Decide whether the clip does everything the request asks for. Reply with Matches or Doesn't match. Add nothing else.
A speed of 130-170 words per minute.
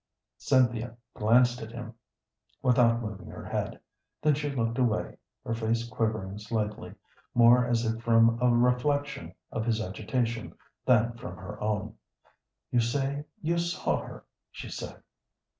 Matches